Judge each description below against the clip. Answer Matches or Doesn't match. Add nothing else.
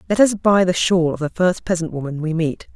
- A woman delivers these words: Matches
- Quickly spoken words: Matches